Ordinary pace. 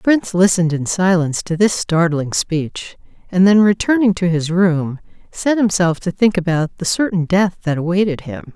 Yes: average, 180 wpm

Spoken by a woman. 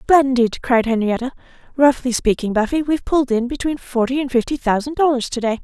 Yes: female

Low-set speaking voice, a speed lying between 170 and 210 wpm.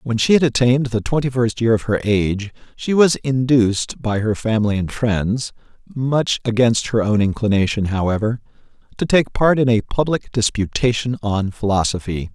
No: low, 115 Hz; average, 155 wpm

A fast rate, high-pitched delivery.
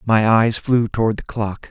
No: fast, 210 wpm; low, 110 Hz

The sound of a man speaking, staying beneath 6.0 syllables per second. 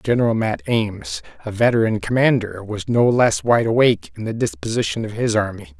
Yes: male; 5.4 syllables/s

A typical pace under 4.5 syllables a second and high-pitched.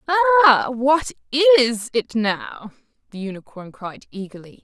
No: 5.1 syllables/s; very high, 255 Hz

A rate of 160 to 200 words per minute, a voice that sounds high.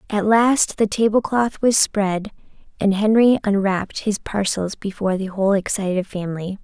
No: average, 145 wpm; high, 205 Hz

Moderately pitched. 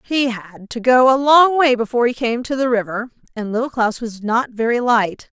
No: high, 240 Hz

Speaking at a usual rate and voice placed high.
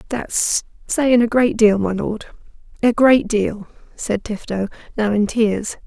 Yes: average, 145 wpm; high, 220 Hz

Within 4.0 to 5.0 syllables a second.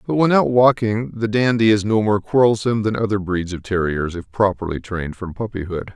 No: 5.6 syllables/s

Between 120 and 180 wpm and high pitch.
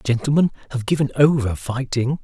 No: slow, 135 wpm; low, 130 Hz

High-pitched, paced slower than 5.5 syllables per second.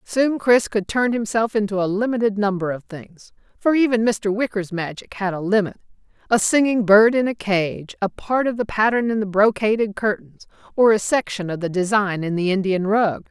Yes: high, 210 Hz; 5.0 syllables/s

